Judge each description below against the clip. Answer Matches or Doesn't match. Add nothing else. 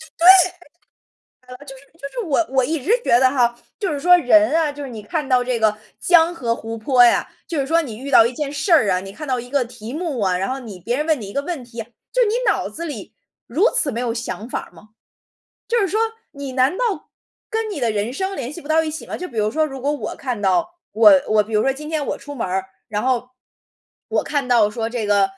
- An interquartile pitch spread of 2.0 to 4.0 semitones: Doesn't match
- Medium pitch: Doesn't match